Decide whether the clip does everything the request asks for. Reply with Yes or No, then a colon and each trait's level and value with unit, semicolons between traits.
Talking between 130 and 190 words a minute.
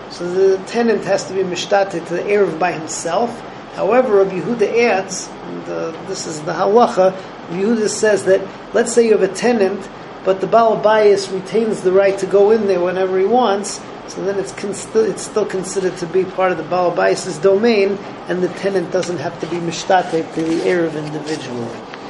No: average, 200 wpm